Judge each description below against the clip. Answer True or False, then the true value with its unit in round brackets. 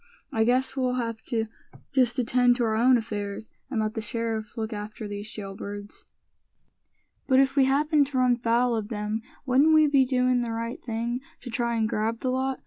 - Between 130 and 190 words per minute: False (200 wpm)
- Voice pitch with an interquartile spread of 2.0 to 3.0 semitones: True (2.7 semitones)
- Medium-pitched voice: False (235 Hz)